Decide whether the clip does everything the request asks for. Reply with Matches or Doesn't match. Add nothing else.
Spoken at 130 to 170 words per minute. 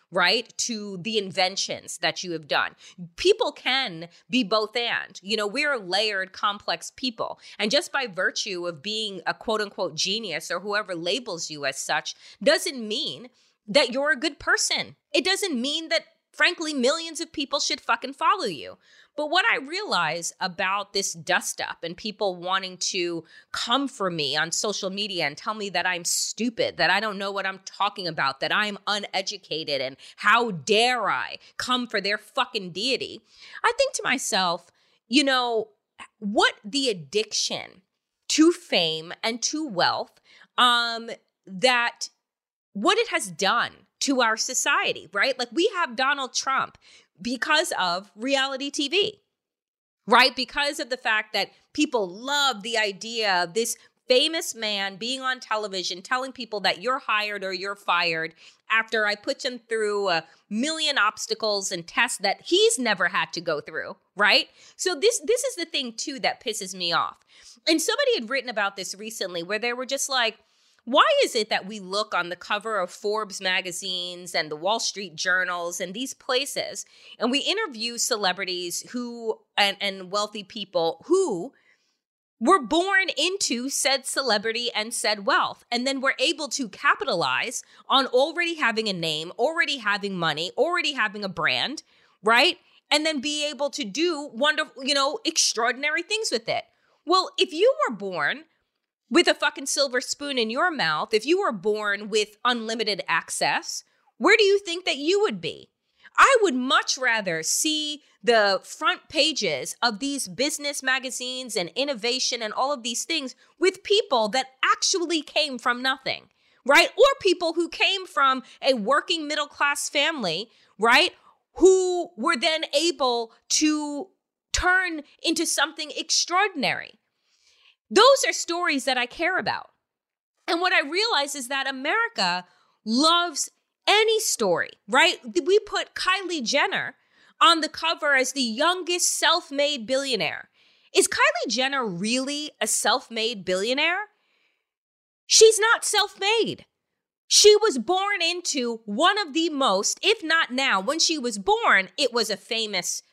Matches